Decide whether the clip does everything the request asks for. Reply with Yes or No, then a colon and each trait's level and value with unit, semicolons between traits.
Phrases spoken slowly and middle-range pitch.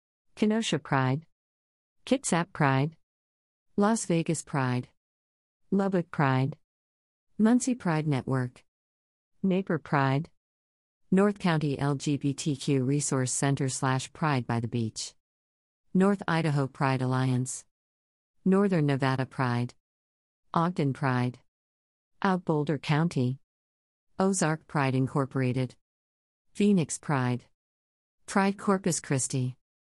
No: slow, 90 wpm; low, 130 Hz